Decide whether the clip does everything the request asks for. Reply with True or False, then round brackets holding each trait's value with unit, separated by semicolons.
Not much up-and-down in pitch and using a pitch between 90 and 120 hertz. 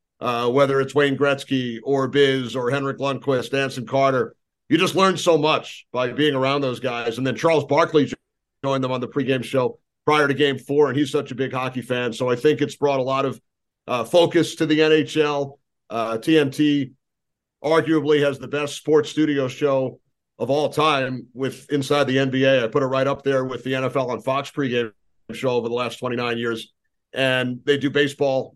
False (2.3 semitones; 135 Hz)